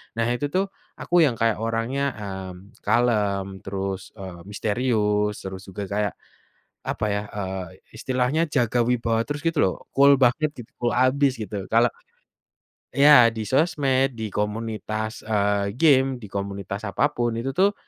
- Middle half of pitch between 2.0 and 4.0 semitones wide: No, average, 4.4 semitones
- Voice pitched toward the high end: No, low, 115 Hz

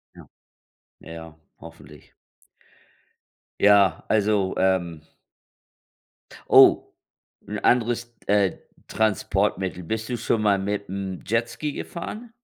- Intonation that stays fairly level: No, average, 3.1 semitones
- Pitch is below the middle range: Yes, low, 100 Hz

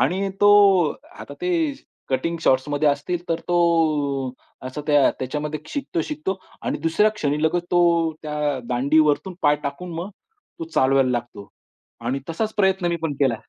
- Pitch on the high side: No, medium, 160 Hz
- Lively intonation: No, average, 4.2 semitones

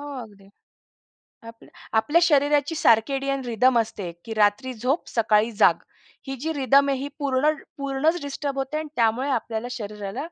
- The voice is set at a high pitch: Yes, very high, 265 Hz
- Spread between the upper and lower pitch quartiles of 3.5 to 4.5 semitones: Yes, average, 4.1 semitones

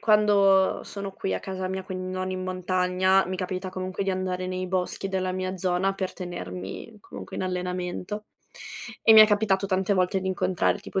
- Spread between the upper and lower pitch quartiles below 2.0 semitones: Yes, narrow, 0.9 semitones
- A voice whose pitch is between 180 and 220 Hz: Yes, medium, 185 Hz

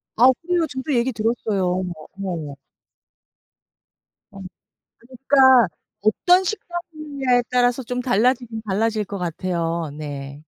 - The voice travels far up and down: Yes, wide, 5.8 semitones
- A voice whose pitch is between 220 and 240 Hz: Yes, high, 235 Hz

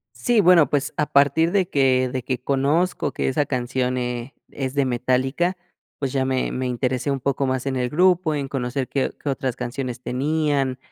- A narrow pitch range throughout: Yes, narrow, 2.3 semitones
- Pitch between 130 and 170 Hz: Yes, low, 135 Hz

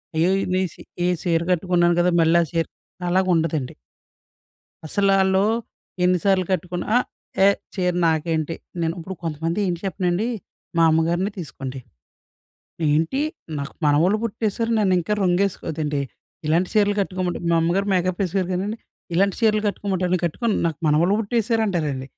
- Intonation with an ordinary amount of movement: Yes, average, 3.0 semitones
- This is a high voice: No, medium, 180 Hz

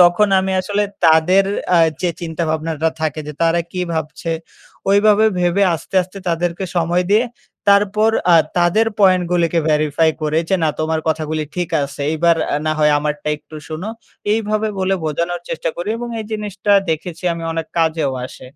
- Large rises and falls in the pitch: No, average, 3.4 semitones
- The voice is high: No, medium, 170 Hz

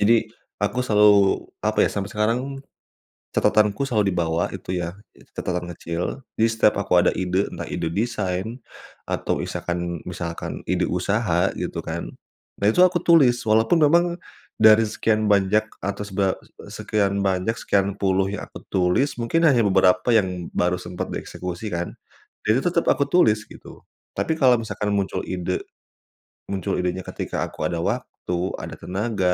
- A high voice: No, low, 100 Hz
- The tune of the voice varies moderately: Yes, average, 3.6 semitones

